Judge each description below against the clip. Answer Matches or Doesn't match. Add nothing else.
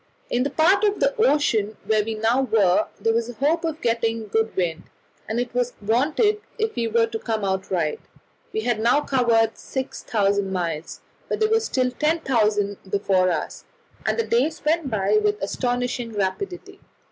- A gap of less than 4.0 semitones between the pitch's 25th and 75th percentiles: Doesn't match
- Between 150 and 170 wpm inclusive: Doesn't match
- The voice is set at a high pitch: Matches